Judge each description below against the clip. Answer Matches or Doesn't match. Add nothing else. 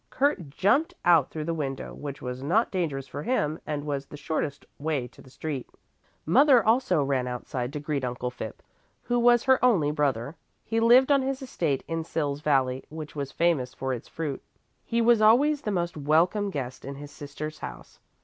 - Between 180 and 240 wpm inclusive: Matches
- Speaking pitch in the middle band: Matches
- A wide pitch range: Matches